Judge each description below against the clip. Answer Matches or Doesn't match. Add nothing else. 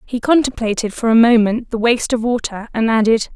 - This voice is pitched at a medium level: Doesn't match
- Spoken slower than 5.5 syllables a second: Doesn't match